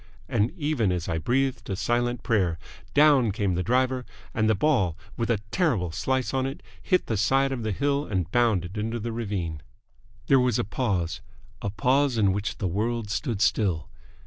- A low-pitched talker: Yes, low, 115 Hz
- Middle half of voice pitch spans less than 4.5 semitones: No, average, 5.1 semitones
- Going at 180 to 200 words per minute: Yes, average, 185 wpm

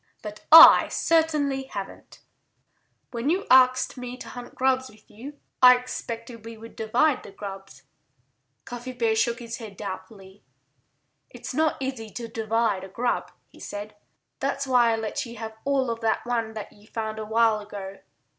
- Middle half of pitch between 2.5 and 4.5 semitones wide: Yes, average, 3.0 semitones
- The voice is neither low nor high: No, high, 230 Hz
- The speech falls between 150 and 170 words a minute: Yes, average, 165 wpm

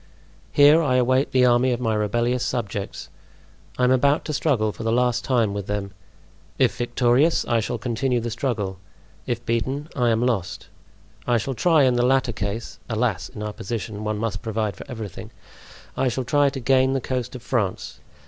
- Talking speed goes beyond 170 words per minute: Yes, average, 185 wpm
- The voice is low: Yes, low, 120 Hz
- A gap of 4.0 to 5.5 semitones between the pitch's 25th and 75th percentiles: No, average, 2.9 semitones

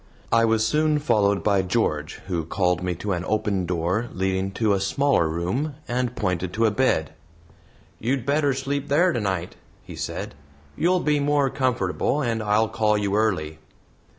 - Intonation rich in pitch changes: Yes, wide, 6.4 semitones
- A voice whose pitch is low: Yes, low, 110 Hz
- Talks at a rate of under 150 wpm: No, average, 165 wpm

